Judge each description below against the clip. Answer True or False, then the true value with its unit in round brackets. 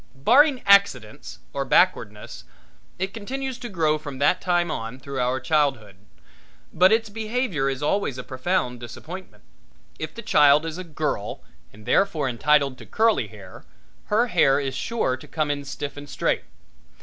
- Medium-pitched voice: True (150 Hz)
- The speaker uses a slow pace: False (160 wpm)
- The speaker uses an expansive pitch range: True (6.9 semitones)